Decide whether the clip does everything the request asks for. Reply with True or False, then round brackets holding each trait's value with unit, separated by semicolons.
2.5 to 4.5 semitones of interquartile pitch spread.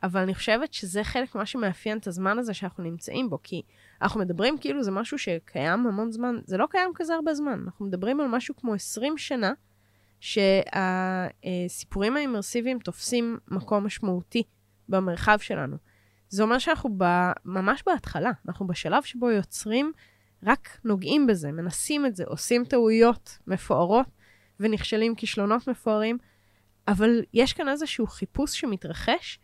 False (4.9 semitones)